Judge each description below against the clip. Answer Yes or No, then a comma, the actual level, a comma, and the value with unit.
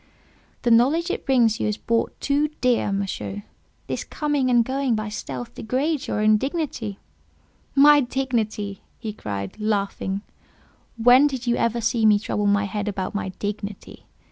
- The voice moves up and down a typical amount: Yes, average, 4.2 semitones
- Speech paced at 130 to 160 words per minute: Yes, average, 155 wpm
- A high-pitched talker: Yes, high, 225 Hz